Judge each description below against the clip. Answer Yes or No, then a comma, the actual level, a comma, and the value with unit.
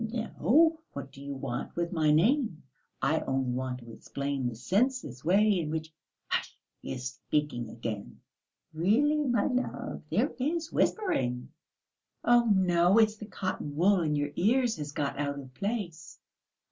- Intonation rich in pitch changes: Yes, wide, 8.3 semitones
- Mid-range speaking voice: Yes, medium, 165 Hz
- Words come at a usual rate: Yes, average, 155 wpm